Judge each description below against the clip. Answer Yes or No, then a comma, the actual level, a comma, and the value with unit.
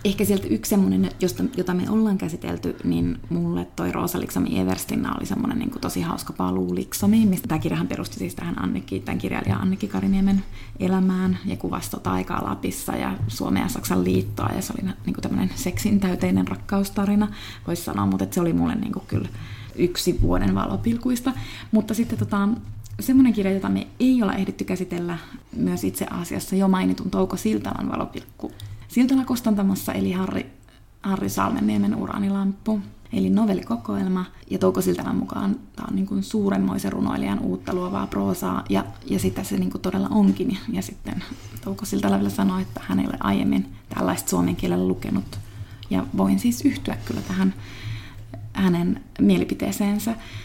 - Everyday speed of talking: No, fast, 160 wpm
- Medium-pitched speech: No, low, 105 Hz